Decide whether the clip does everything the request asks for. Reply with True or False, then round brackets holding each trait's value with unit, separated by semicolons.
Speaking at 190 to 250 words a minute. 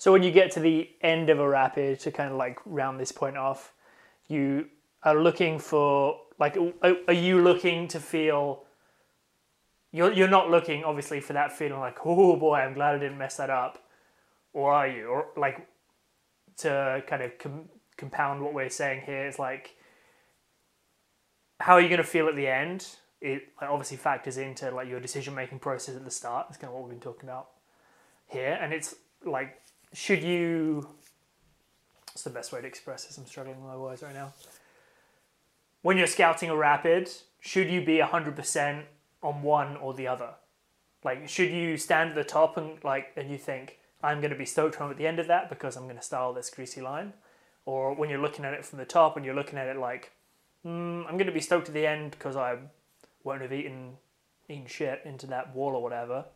True (200 wpm)